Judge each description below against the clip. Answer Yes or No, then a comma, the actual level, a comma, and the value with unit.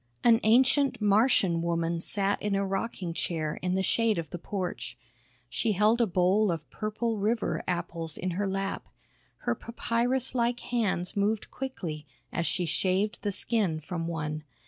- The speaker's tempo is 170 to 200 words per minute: No, average, 160 wpm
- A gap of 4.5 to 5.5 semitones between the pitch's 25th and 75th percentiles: Yes, average, 4.8 semitones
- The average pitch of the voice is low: No, high, 195 Hz